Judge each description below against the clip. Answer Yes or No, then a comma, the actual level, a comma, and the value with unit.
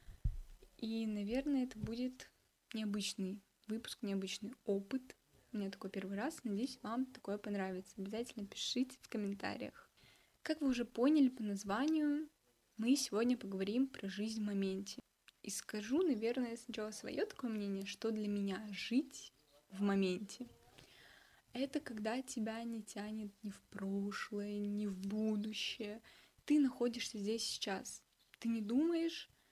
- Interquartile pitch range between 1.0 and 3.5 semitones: No, average, 3.9 semitones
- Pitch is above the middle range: Yes, high, 220 Hz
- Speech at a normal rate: Yes, average, 130 wpm